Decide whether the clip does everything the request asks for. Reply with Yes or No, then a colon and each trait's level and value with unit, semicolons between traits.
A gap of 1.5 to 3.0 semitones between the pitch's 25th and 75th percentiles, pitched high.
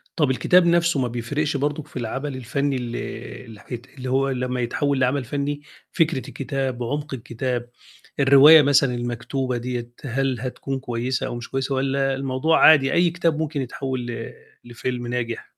No: narrow, 2.5 semitones; low, 130 Hz